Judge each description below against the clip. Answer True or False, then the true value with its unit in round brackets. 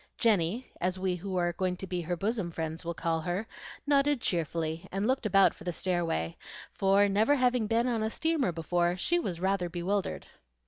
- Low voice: False (185 Hz)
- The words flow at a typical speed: True (190 wpm)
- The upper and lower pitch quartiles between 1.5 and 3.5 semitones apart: False (4.2 semitones)